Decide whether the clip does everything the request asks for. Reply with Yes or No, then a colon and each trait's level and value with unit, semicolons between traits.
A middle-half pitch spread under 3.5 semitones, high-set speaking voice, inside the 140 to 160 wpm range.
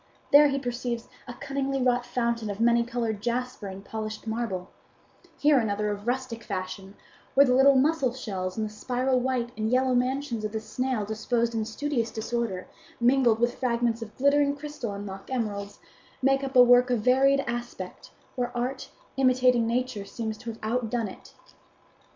No: average, 2.8 semitones; high, 240 Hz; average, 170 wpm